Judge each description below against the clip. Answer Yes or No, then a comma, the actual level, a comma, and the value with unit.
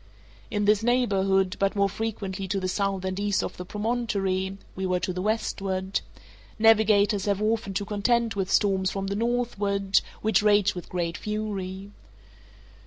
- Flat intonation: Yes, narrow, 2.0 semitones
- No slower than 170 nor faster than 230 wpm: No, average, 160 wpm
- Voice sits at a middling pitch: No, high, 200 Hz